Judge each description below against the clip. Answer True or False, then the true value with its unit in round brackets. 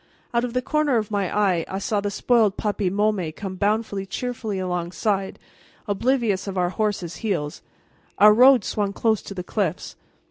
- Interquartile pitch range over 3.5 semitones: False (2.7 semitones)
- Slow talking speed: False (170 wpm)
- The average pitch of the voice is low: False (205 Hz)